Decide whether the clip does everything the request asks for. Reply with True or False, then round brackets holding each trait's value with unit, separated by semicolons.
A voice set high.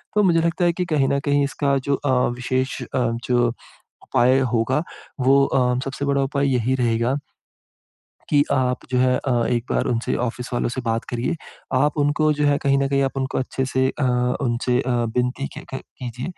False (130 Hz)